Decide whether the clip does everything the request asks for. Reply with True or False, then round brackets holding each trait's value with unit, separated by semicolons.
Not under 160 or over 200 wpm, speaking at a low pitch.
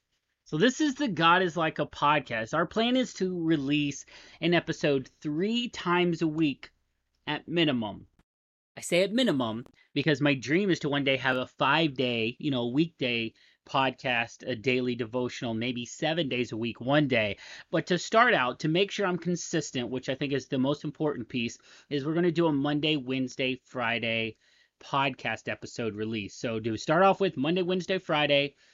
False (185 wpm; 145 Hz)